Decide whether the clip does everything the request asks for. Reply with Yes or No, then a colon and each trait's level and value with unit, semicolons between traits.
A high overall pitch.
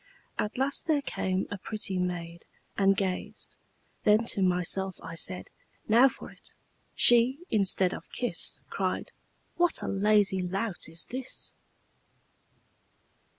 Yes: high, 195 Hz